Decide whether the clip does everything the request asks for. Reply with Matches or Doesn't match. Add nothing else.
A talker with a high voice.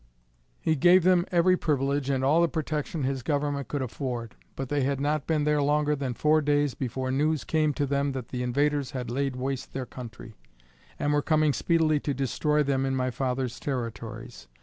Doesn't match